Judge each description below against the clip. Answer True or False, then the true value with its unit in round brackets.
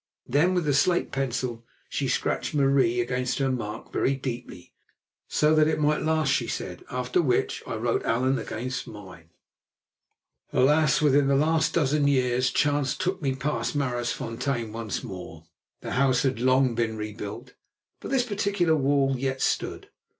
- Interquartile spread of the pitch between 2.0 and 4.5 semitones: True (3.5 semitones)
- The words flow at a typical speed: True (155 wpm)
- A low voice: True (130 Hz)